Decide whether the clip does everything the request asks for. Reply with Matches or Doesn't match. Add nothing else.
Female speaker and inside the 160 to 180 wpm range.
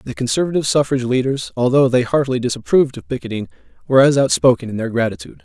Doesn't match